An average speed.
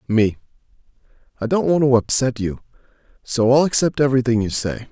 Yes: average, 160 wpm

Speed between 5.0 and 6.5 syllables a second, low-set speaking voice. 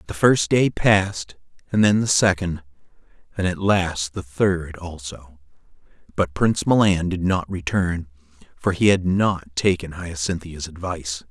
No: 4.3 syllables/s; very low, 90 Hz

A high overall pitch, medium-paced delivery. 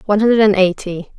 Yes: high, 200 Hz; average, 150 wpm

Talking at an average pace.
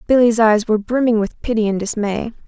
Yes: average, 195 wpm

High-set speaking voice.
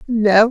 Yes: high, 220 Hz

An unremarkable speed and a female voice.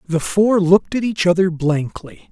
No: average, 180 wpm; male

